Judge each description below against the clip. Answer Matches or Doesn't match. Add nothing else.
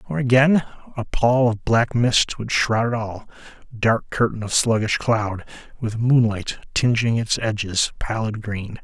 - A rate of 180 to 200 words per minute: Doesn't match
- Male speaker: Matches